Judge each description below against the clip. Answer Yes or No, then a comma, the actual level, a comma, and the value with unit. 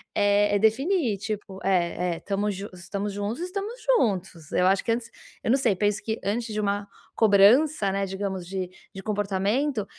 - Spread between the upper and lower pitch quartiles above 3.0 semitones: No, narrow, 2.6 semitones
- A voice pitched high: Yes, high, 205 Hz